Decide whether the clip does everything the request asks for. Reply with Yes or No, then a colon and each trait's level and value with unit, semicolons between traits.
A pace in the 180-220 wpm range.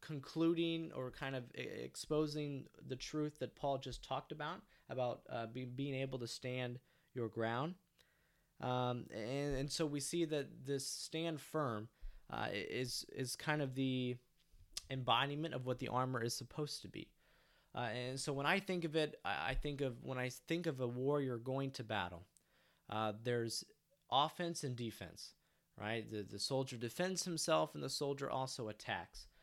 No: average, 165 wpm